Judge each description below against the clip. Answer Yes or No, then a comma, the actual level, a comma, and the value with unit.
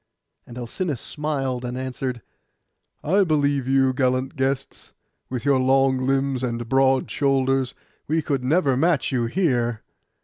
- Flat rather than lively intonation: Yes, narrow, 1.7 semitones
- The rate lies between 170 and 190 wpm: No, slow, 135 wpm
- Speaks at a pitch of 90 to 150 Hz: Yes, low, 135 Hz